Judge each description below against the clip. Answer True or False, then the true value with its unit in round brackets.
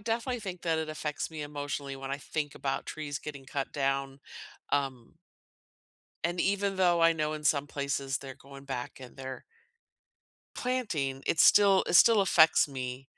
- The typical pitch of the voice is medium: True (145 Hz)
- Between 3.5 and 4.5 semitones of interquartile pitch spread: True (4.1 semitones)